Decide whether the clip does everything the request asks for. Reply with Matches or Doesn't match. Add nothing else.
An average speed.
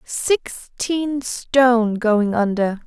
Doesn't match